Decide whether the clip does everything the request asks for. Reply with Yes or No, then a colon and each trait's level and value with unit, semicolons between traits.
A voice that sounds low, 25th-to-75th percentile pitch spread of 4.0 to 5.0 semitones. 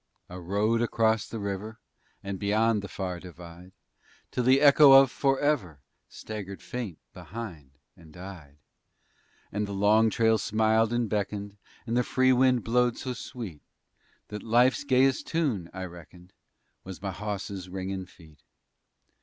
Yes: low, 105 Hz; average, 4.3 semitones